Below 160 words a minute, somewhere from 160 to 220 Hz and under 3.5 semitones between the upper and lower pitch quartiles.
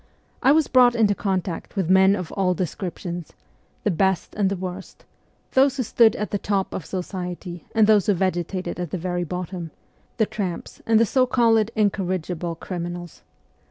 No: average, 170 wpm; high, 190 Hz; average, 3.1 semitones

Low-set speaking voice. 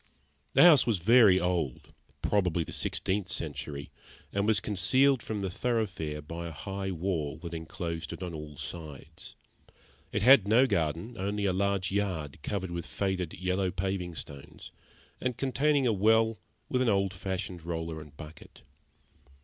Yes: very low, 95 Hz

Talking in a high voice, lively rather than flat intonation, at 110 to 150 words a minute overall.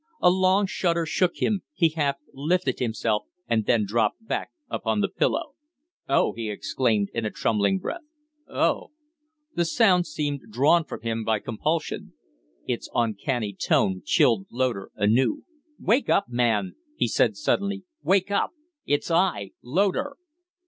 No: low, 135 Hz; wide, 8.5 semitones; average, 140 wpm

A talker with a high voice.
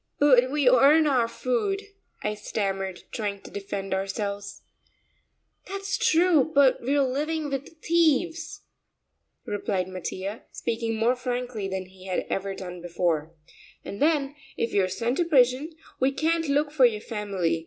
Yes: high, 245 Hz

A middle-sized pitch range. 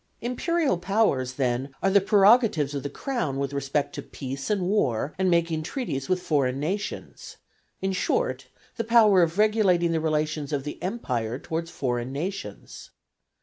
No: wide, 6.5 semitones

